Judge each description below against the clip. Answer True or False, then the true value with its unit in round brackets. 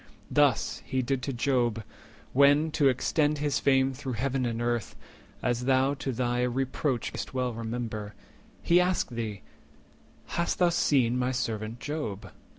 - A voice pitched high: False (125 Hz)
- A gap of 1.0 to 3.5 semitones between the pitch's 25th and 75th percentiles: True (2.9 semitones)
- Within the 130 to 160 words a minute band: True (150 wpm)